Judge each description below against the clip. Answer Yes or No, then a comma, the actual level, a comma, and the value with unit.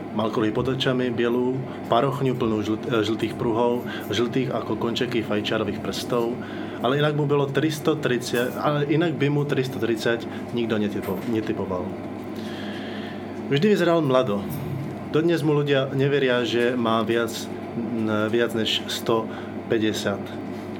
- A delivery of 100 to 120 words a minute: Yes, slow, 115 wpm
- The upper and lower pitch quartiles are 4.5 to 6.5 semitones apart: No, average, 3.0 semitones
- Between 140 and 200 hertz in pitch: No, low, 120 Hz